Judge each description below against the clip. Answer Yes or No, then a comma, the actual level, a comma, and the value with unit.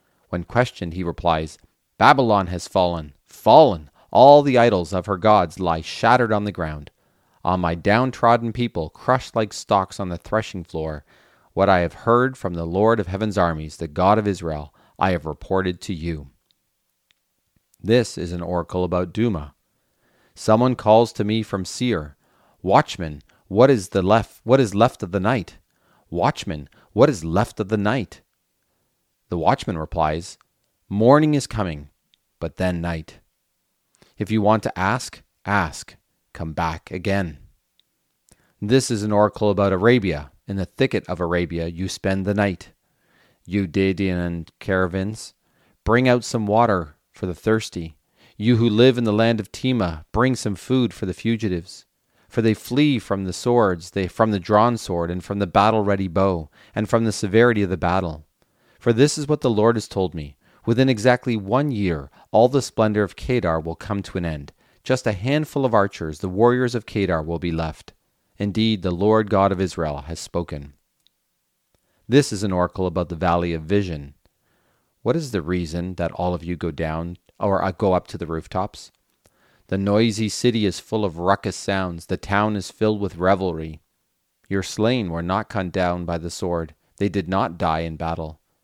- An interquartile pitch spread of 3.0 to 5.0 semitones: Yes, average, 4.3 semitones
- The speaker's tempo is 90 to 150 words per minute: No, average, 175 wpm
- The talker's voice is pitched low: Yes, very low, 95 Hz